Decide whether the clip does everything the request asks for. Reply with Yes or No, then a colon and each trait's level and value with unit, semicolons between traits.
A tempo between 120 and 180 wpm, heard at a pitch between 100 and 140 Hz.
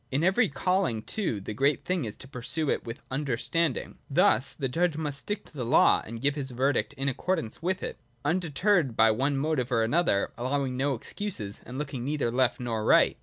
No: average, 200 wpm; low, 135 Hz